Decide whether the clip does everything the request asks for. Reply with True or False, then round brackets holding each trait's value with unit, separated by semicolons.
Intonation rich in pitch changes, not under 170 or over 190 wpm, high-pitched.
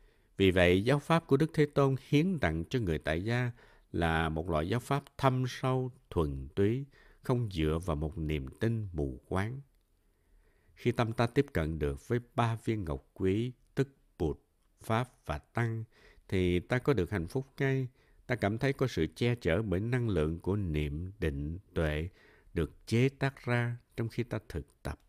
False (7.5 semitones; 185 wpm; 105 Hz)